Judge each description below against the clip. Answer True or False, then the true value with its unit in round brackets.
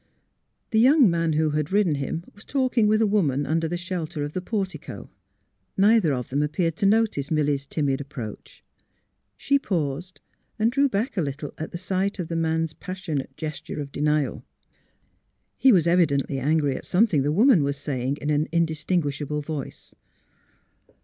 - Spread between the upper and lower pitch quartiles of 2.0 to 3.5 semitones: False (4.9 semitones)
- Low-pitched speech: False (160 Hz)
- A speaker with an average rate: True (170 wpm)